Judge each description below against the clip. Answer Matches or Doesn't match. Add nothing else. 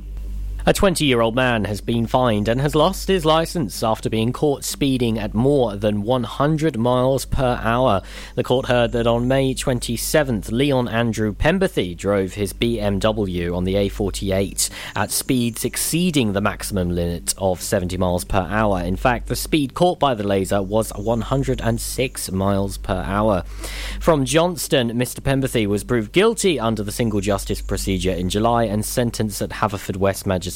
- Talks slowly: Doesn't match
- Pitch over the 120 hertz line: Doesn't match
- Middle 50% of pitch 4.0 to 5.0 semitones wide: Matches